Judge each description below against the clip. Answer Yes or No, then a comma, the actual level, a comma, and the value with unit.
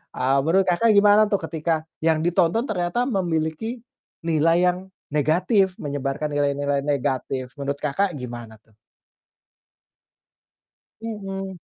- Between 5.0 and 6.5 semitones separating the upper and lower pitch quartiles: Yes, average, 5.3 semitones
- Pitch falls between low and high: Yes, medium, 160 Hz